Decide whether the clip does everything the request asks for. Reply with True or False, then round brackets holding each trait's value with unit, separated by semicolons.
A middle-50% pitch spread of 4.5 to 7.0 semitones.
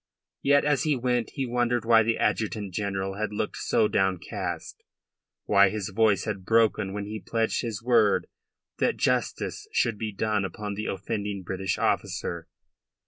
False (2.7 semitones)